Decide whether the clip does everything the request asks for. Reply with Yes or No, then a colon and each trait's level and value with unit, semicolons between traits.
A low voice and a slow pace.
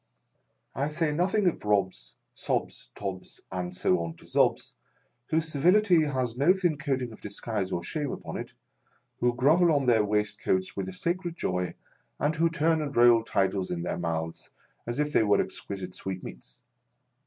No: low, 120 Hz; average, 170 wpm